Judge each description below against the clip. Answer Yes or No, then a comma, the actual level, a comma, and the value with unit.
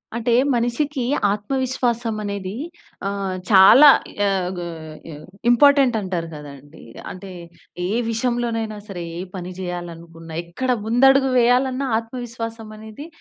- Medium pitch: No, high, 220 Hz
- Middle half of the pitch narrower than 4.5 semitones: No, average, 4.8 semitones